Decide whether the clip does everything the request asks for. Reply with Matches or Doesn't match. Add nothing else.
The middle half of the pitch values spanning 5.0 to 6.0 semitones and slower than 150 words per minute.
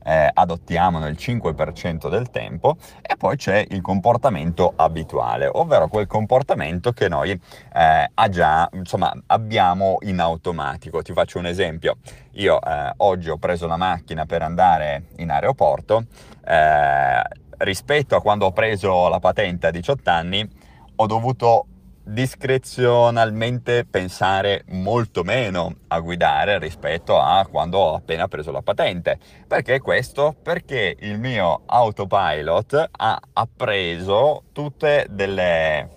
Matches